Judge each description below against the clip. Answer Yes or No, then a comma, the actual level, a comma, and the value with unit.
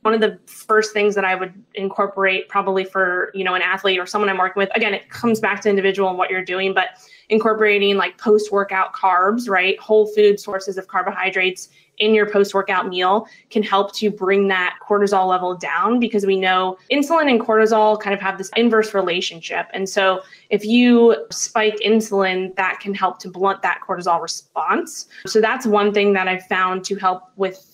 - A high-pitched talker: Yes, high, 195 Hz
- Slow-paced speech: No, average, 195 wpm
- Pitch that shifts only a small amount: Yes, narrow, 2.1 semitones